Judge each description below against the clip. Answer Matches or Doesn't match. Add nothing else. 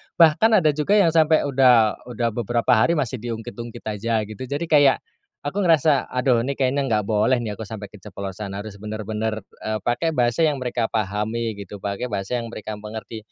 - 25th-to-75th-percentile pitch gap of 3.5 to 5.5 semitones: Matches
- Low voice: Matches